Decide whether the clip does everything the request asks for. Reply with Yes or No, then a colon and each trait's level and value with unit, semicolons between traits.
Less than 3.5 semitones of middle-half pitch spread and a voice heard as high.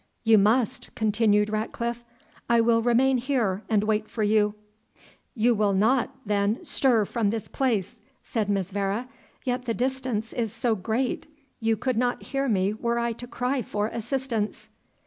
Yes: average, 2.7 semitones; high, 225 Hz